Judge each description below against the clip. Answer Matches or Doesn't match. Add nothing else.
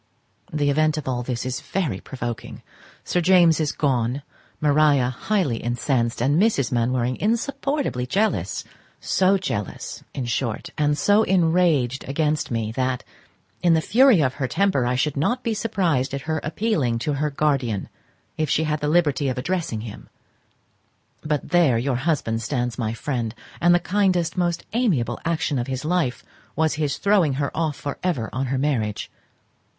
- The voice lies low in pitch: Doesn't match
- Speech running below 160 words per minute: Doesn't match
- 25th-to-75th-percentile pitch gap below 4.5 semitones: Doesn't match